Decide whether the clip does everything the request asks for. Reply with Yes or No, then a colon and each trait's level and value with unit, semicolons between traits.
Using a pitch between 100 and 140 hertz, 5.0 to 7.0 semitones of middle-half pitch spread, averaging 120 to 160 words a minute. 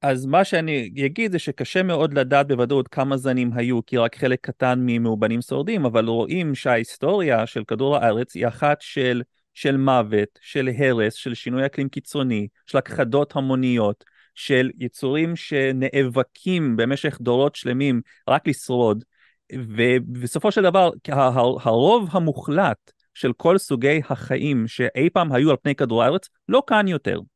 No: low, 135 Hz; average, 3.0 semitones; average, 145 wpm